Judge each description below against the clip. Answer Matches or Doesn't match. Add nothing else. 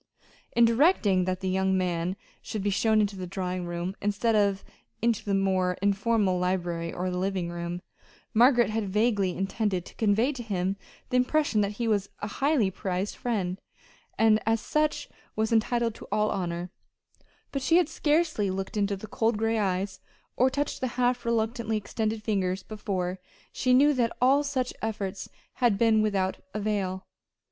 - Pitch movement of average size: Matches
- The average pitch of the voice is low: Doesn't match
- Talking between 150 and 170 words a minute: Matches